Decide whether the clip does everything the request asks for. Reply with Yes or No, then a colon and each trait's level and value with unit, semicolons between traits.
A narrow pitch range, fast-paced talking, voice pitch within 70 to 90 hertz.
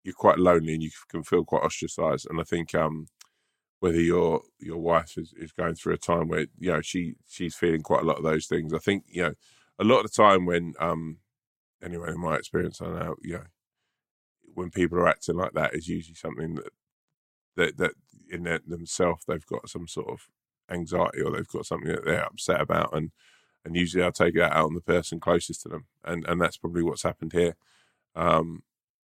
Yes: narrow, 1.5 semitones; fast, 215 wpm; very low, 85 Hz